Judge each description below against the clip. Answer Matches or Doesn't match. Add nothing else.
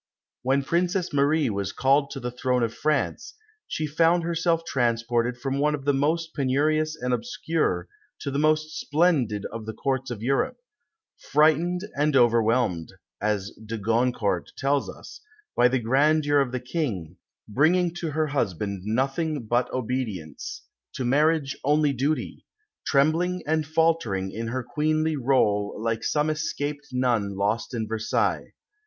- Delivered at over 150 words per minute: Doesn't match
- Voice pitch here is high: Doesn't match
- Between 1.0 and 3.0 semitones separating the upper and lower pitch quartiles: Doesn't match